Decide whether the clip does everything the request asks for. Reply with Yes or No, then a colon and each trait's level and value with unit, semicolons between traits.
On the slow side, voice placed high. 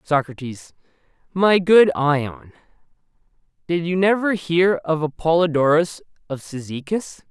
No: slow, 100 wpm; medium, 165 Hz